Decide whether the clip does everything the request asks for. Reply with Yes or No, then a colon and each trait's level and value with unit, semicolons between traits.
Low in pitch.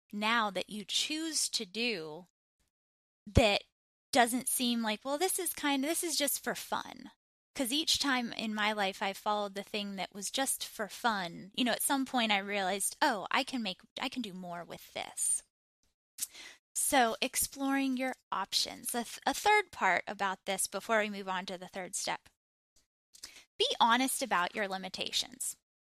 No: high, 220 Hz